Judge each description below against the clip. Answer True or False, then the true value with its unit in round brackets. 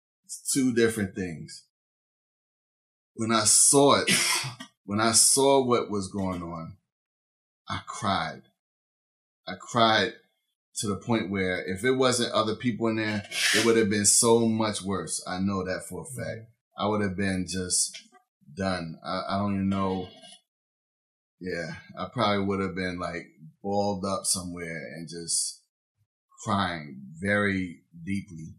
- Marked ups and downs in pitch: False (3.5 semitones)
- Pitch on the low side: True (100 Hz)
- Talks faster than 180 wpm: False (145 wpm)